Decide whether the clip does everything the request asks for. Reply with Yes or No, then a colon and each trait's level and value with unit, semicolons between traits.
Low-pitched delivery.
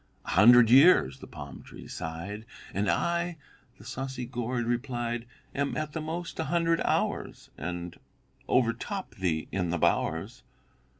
Yes: low, 120 Hz